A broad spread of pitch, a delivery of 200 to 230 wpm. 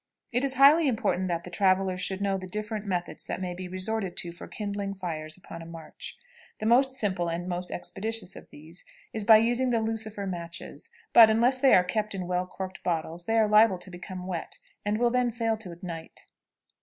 No: average, 3.8 semitones; fast, 205 wpm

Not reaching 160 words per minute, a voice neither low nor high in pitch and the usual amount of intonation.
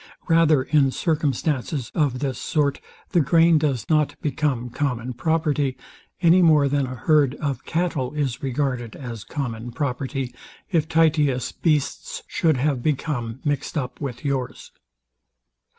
Yes: slow, 135 wpm; medium, 145 Hz; average, 3.4 semitones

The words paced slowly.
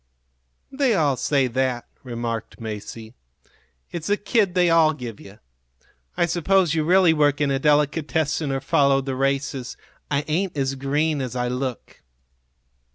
No: average, 150 wpm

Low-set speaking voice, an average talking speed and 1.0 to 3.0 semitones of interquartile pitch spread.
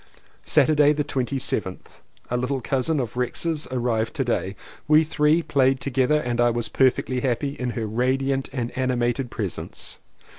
Yes: low, 130 Hz; average, 155 wpm; average, 2.7 semitones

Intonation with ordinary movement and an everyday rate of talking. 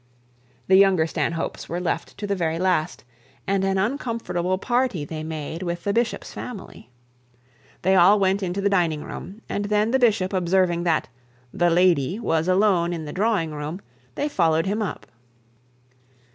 Yes: average, 3.3 semitones; average, 160 wpm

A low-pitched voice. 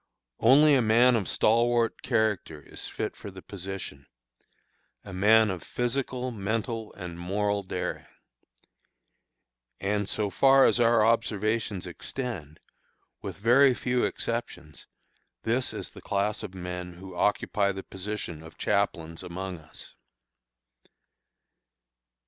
Yes: low, 105 Hz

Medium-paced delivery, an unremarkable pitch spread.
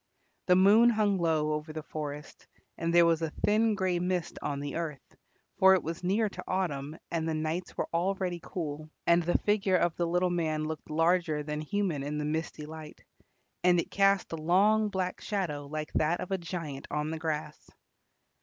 Yes: average, 190 wpm; average, 3.3 semitones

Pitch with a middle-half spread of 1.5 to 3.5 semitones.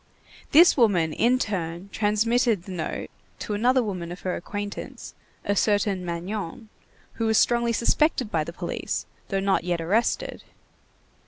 No: average, 4.5 semitones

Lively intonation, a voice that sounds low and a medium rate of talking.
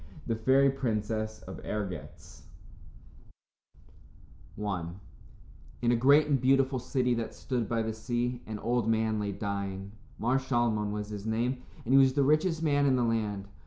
No: average, 3.7 semitones; low, 115 Hz; average, 160 wpm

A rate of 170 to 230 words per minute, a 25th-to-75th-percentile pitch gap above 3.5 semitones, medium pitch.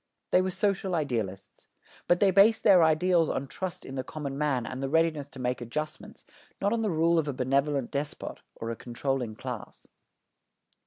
Yes: average, 180 wpm; average, 5.2 semitones; medium, 150 Hz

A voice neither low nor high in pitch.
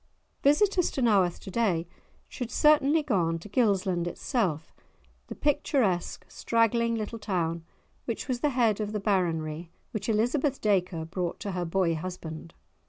No: high, 205 Hz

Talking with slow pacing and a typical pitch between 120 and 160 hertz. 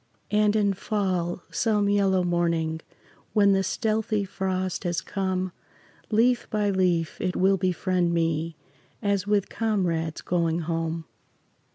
No: slow, 125 wpm; medium, 185 Hz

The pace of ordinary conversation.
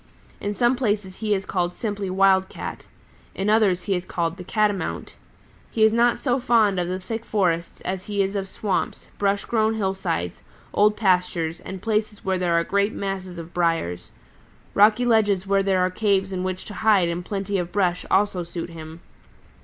Yes: average, 185 wpm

